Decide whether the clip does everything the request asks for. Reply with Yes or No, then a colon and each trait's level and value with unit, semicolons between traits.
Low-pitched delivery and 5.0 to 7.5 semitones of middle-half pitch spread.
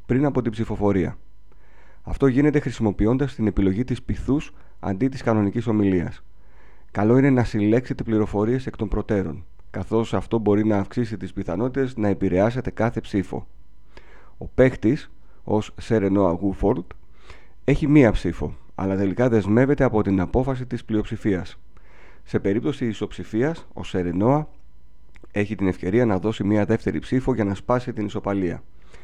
No: low, 105 Hz; average, 4.1 semitones